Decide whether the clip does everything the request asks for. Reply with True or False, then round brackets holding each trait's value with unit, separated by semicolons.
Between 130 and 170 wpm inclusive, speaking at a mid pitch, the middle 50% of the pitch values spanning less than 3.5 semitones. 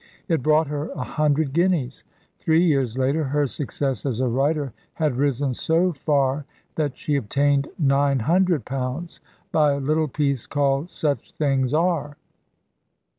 True (145 wpm; 145 Hz; 2.4 semitones)